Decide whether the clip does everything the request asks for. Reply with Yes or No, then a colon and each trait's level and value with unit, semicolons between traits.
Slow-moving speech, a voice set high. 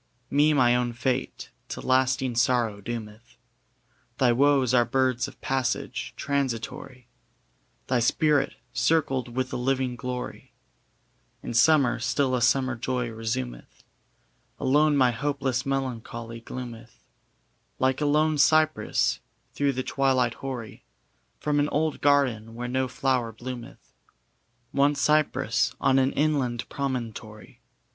No: slow, 120 wpm; low, 130 Hz